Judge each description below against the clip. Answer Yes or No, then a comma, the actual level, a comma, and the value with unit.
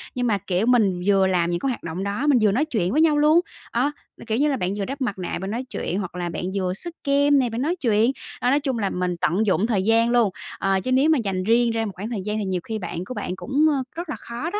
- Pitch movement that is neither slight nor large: No, wide, 5.8 semitones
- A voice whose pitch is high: Yes, high, 225 Hz